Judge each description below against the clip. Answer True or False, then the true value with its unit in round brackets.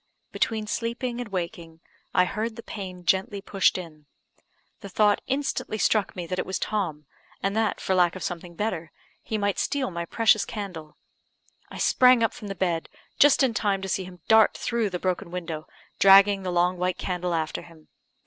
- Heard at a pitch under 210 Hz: True (190 Hz)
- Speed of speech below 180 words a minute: False (185 wpm)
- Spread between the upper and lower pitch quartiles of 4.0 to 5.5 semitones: False (3.6 semitones)